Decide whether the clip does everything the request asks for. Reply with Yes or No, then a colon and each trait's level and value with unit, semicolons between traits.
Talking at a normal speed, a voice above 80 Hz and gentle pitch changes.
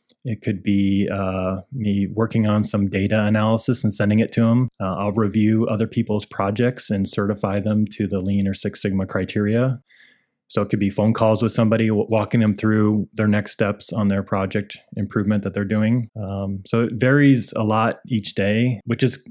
Yes: average, 195 wpm; low, 105 Hz; narrow, 2.1 semitones